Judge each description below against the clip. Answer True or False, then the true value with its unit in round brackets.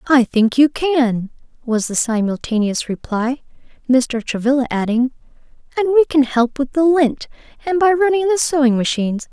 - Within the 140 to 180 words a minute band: True (155 wpm)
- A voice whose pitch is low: False (265 Hz)